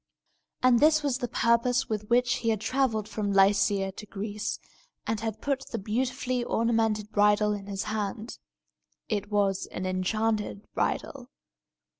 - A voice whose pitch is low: No, high, 215 Hz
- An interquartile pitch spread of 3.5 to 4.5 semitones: No, average, 2.9 semitones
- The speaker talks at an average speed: Yes, average, 145 wpm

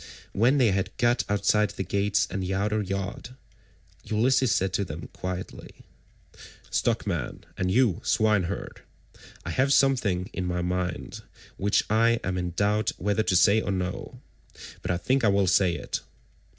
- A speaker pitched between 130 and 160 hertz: No, low, 100 Hz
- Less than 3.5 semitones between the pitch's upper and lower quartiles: Yes, average, 3.1 semitones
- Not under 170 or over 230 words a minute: No, average, 155 wpm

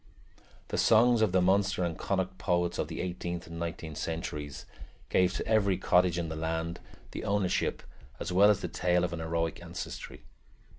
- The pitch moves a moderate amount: No, narrow, 2.3 semitones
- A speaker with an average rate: Yes, average, 180 wpm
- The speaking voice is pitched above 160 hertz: No, very low, 90 Hz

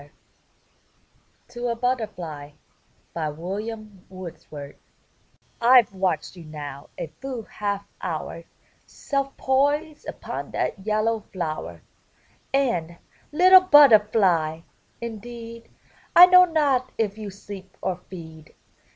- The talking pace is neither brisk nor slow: No, slow, 100 wpm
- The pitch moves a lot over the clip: Yes, wide, 6.7 semitones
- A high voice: Yes, high, 210 Hz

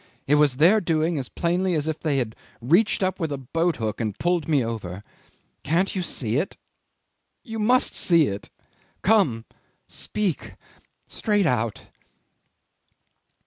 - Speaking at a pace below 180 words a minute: Yes, average, 145 wpm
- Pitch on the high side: No, medium, 155 Hz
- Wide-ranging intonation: Yes, wide, 7.1 semitones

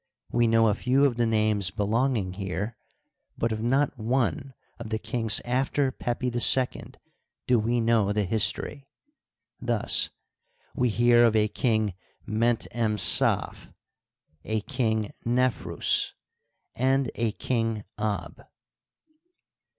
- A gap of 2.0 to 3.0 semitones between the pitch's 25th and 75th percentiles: Yes, narrow, 2.6 semitones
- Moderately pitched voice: No, low, 115 Hz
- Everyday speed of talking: No, slow, 120 wpm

